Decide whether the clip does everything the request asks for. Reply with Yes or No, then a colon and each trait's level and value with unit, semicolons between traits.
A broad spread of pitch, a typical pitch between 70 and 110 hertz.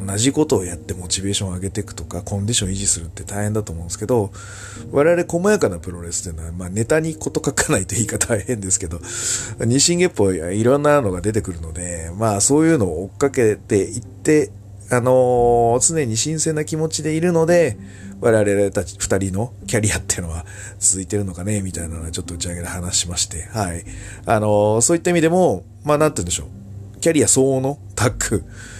No: average, 4.9 semitones; low, 105 Hz